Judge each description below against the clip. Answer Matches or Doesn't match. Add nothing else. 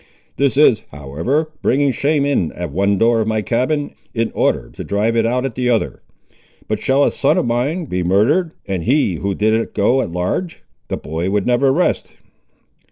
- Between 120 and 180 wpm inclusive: Doesn't match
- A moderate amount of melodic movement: Doesn't match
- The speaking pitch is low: Matches